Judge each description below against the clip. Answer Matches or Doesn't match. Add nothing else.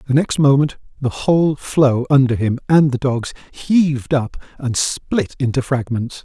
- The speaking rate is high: Doesn't match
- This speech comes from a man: Matches